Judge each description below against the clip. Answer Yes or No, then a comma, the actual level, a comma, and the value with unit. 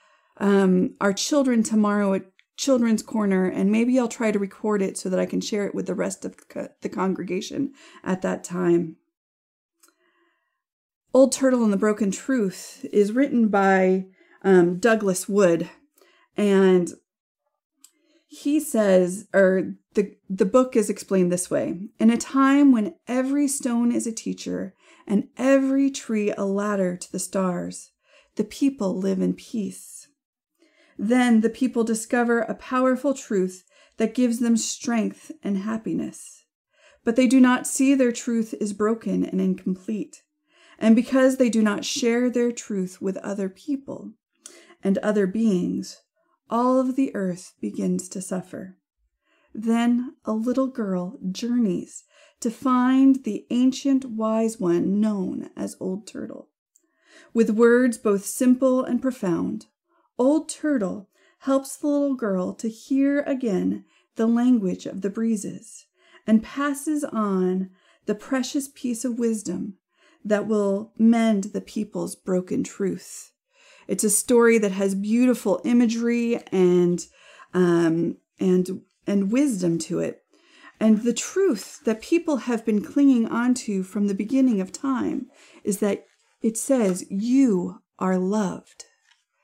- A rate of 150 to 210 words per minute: No, average, 140 wpm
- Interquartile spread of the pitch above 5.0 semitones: Yes, wide, 5.5 semitones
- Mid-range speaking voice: No, high, 225 Hz